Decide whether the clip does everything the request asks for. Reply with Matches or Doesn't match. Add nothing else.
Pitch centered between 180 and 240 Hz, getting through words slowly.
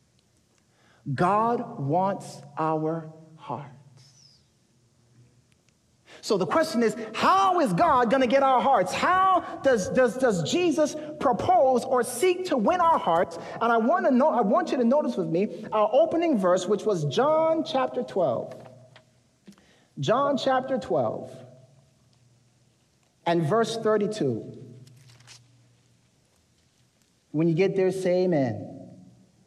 Matches